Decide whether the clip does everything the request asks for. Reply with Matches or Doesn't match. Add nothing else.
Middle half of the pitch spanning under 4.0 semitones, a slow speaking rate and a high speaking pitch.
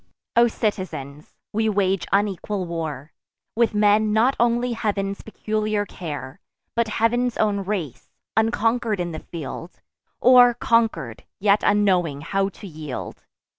Doesn't match